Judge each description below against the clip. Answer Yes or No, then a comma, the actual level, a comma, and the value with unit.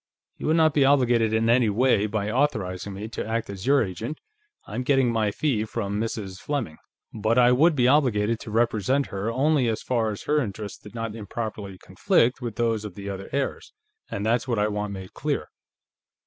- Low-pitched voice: Yes, low, 115 Hz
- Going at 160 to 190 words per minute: No, average, 200 wpm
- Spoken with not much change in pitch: No, average, 3.5 semitones